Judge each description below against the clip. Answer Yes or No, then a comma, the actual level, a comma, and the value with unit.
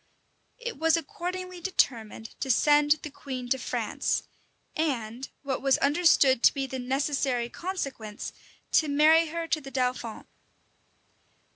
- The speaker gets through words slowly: Yes, slow, 130 wpm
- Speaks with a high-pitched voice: Yes, very high, 280 Hz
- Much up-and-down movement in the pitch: No, average, 4.3 semitones